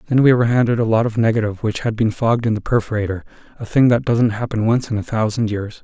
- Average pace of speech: No, fast, 255 wpm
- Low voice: Yes, low, 115 Hz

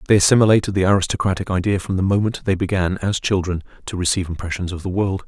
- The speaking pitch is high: No, very low, 95 Hz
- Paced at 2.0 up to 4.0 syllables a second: No, 7.0 syllables/s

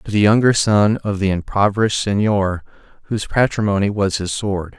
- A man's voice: Yes, male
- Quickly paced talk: No, average, 165 wpm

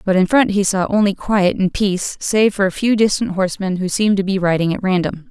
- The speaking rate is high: Yes, fast, 250 wpm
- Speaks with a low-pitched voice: No, high, 195 Hz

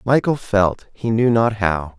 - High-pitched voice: No, low, 110 Hz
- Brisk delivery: No, average, 180 wpm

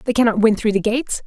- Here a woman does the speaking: Yes, female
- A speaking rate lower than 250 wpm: No, fast, 285 wpm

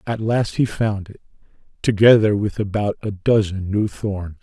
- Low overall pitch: Yes, low, 105 Hz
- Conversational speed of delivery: Yes, average, 165 wpm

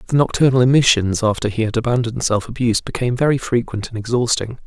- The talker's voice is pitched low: Yes, low, 120 Hz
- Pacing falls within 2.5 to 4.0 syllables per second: No, 6.9 syllables/s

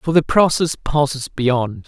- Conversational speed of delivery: Yes, average, 160 wpm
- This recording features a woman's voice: No, male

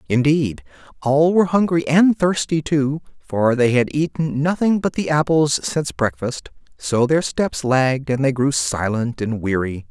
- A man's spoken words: Yes, male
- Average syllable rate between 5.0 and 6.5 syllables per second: No, 4.4 syllables/s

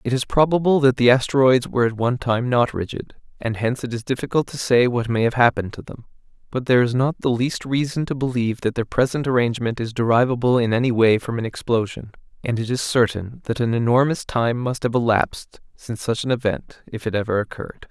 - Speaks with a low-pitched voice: Yes, low, 120 Hz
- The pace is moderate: No, fast, 220 wpm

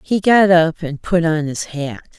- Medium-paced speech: No, fast, 220 wpm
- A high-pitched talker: No, medium, 165 Hz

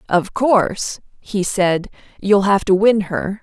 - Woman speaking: Yes, female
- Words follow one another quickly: No, average, 160 wpm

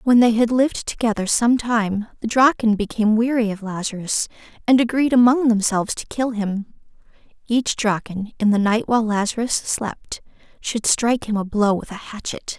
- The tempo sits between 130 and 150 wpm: No, average, 170 wpm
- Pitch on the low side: No, high, 225 Hz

